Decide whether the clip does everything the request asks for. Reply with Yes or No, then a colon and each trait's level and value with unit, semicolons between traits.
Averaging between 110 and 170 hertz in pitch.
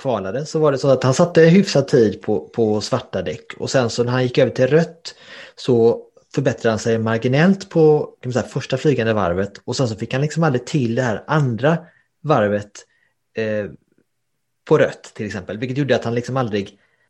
Yes: low, 130 Hz